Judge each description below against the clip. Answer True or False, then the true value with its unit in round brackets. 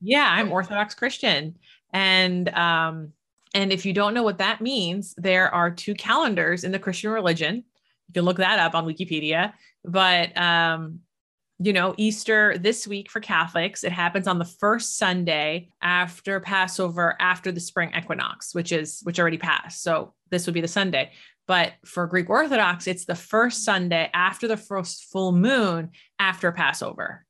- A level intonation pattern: False (3.0 semitones)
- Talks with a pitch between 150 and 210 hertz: True (185 Hz)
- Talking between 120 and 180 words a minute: True (165 wpm)